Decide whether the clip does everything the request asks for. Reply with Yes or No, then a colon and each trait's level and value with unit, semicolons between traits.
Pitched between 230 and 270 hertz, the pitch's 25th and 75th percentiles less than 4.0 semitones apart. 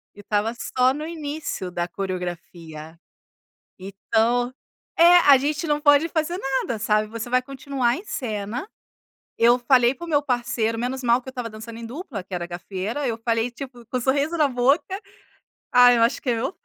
No: high, 245 Hz; average, 4.3 semitones